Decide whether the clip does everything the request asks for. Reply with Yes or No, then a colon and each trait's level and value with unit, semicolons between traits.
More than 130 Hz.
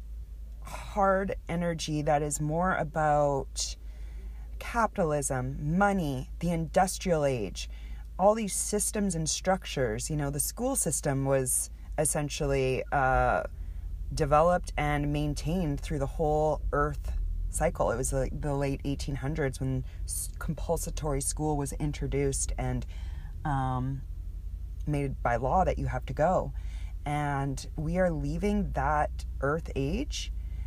Yes: medium, 140 Hz